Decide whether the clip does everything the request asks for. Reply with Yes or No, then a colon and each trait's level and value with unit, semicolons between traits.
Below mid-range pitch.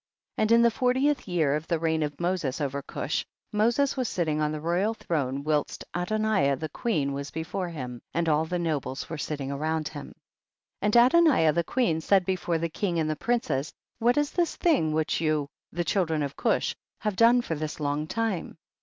No: medium, 165 Hz